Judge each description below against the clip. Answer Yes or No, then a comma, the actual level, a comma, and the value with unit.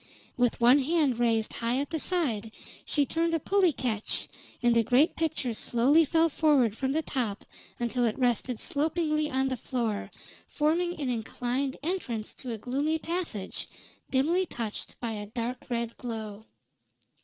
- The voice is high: Yes, very high, 255 Hz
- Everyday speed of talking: Yes, average, 155 wpm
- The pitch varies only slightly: No, average, 5.0 semitones